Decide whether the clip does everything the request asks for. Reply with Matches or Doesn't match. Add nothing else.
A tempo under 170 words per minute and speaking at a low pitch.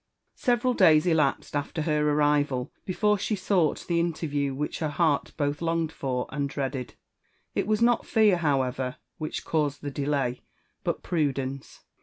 Doesn't match